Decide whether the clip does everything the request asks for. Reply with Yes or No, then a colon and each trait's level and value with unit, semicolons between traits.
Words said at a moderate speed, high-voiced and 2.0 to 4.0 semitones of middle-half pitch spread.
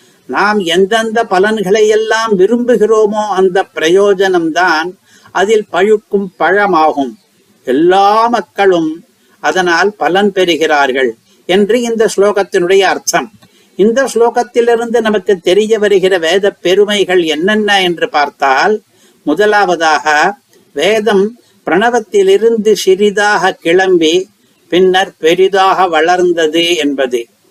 Yes: average, 85 wpm; high, 195 Hz; average, 3.2 semitones